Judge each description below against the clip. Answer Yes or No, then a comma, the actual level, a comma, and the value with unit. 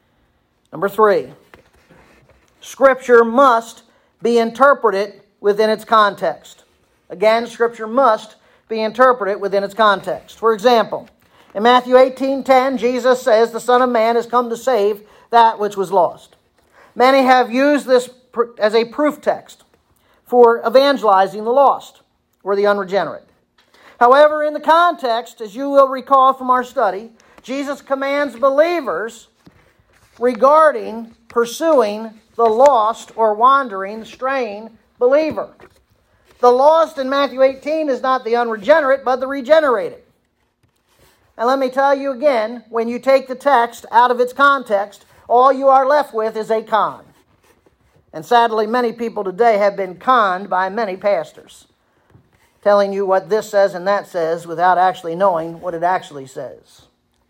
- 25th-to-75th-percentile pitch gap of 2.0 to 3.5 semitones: No, average, 3.9 semitones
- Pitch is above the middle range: Yes, high, 235 Hz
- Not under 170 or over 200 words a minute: No, average, 140 wpm